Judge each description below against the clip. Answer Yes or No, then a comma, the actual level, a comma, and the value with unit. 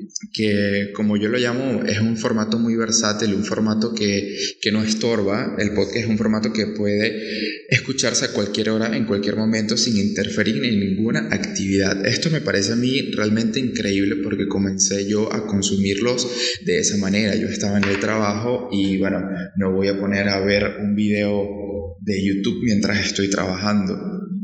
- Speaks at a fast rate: No, average, 170 wpm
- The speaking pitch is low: Yes, low, 105 Hz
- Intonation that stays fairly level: Yes, narrow, 2.1 semitones